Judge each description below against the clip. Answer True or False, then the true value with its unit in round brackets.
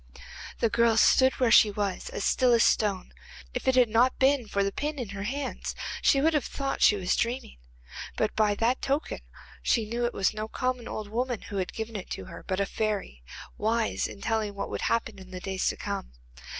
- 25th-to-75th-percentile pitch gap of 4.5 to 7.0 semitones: False (4.0 semitones)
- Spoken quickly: True (220 wpm)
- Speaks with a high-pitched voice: True (225 Hz)